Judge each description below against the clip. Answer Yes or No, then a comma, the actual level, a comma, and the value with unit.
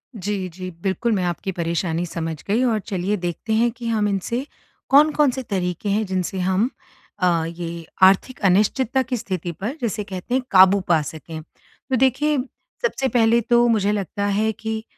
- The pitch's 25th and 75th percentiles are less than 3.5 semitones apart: No, average, 4.7 semitones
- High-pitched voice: Yes, high, 200 Hz